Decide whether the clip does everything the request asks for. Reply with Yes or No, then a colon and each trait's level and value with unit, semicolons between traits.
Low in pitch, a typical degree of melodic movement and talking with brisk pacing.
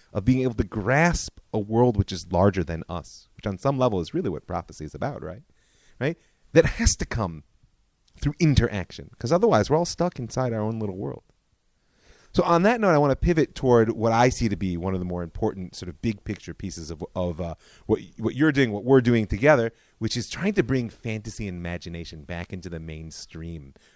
No: low, 110 Hz; wide, 6.5 semitones; fast, 220 wpm